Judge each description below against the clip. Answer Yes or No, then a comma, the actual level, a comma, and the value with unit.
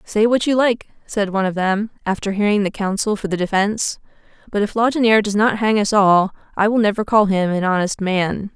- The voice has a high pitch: Yes, high, 205 Hz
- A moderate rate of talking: No, fast, 215 wpm